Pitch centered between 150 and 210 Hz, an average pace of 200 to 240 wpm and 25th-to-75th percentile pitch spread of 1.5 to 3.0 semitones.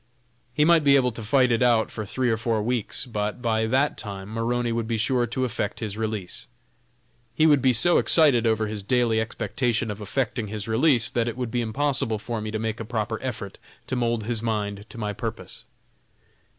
No: low, 115 Hz; fast, 205 wpm; narrow, 2.4 semitones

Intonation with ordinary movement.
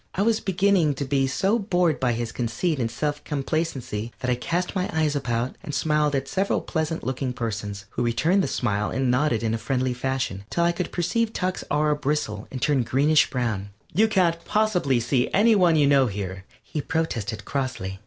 No: wide, 5.9 semitones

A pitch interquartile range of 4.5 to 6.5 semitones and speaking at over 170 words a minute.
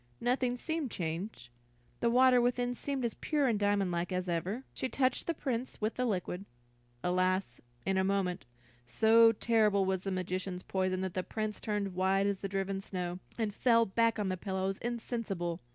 No: average, 4.0 semitones; average, 180 wpm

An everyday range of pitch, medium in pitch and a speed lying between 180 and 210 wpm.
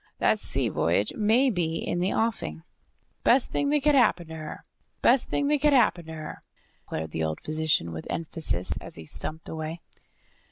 No: wide, 7.7 semitones; medium, 165 Hz; average, 185 wpm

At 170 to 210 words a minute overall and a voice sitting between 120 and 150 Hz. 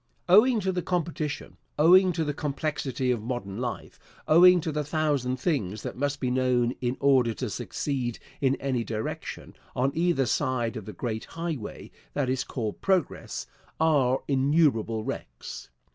No: average, 155 wpm; low, 135 Hz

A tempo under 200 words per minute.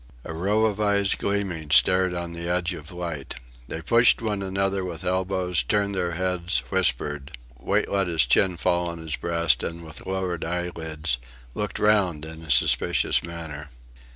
Yes: average, 165 wpm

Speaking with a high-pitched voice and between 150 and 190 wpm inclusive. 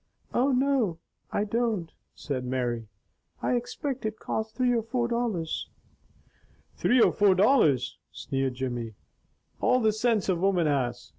No: high, 210 Hz; average, 140 wpm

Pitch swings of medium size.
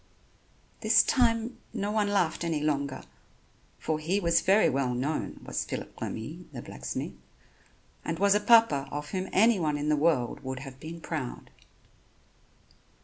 No: wide, 6.0 semitones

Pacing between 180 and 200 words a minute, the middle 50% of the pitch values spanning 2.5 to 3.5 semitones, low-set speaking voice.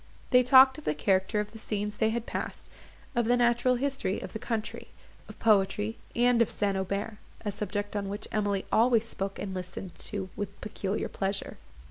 No: average, 185 wpm; average, 2.9 semitones; high, 210 Hz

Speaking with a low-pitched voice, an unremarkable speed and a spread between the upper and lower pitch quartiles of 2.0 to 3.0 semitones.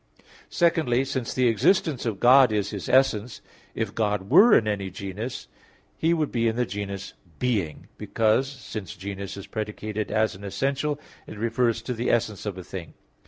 No: low, 110 Hz; average, 165 wpm; average, 4.1 semitones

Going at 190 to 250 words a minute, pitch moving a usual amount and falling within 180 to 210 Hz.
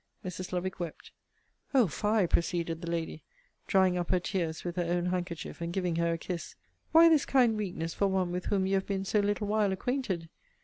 Yes: fast, 205 wpm; average, 3.0 semitones; medium, 185 Hz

